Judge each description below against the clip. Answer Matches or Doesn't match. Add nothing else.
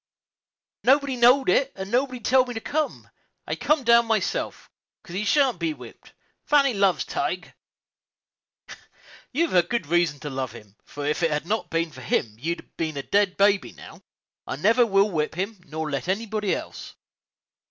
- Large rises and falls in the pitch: Matches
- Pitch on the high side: Matches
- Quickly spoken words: Doesn't match